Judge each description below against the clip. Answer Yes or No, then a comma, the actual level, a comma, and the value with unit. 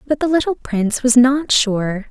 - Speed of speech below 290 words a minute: Yes, average, 200 wpm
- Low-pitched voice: No, very high, 250 Hz